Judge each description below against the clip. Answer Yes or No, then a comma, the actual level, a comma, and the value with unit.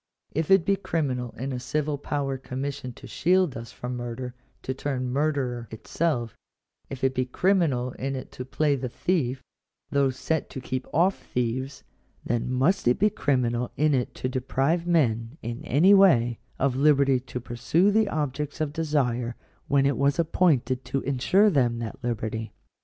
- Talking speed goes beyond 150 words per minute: Yes, average, 170 wpm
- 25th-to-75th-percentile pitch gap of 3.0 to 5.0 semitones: Yes, average, 3.6 semitones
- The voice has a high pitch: No, low, 135 Hz